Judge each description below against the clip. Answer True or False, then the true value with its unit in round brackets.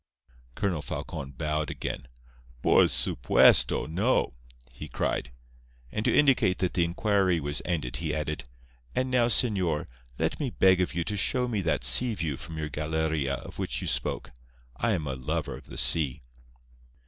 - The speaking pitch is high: False (85 Hz)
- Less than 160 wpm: False (165 wpm)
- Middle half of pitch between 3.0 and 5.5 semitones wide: True (5.2 semitones)